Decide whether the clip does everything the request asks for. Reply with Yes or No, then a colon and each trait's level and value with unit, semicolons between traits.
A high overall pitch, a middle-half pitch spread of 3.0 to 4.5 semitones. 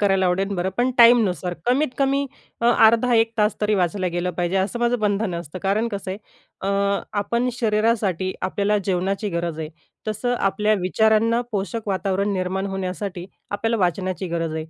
Yes: high, 200 Hz; average, 3.3 semitones